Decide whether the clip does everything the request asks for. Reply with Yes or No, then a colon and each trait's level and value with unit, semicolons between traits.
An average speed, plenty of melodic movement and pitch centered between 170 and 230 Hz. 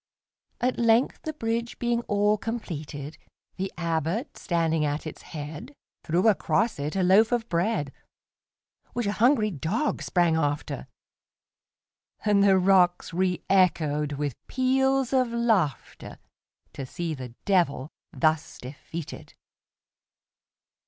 No: slow, 100 wpm; wide, 6.5 semitones; medium, 185 Hz